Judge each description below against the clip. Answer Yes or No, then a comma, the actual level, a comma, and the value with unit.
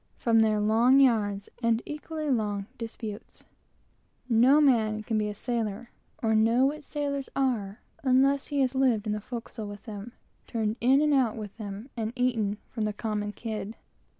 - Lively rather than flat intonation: No, average, 3.6 semitones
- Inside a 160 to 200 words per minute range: Yes, average, 180 wpm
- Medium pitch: No, high, 230 Hz